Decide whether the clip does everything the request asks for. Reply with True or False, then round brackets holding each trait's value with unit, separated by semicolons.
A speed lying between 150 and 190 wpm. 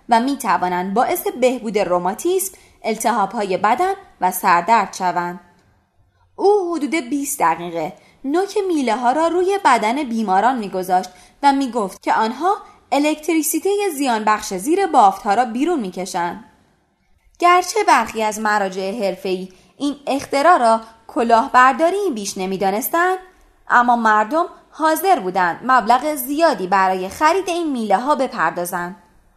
False (120 wpm)